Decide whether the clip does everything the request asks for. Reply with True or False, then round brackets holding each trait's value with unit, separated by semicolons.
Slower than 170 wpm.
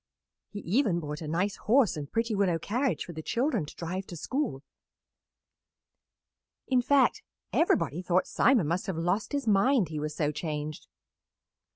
True (160 wpm)